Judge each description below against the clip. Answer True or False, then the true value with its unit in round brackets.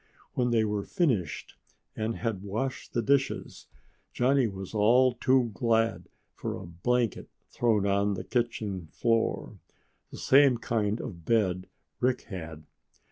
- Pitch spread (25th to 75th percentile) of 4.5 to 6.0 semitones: False (3.6 semitones)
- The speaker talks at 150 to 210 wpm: False (135 wpm)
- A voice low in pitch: True (115 Hz)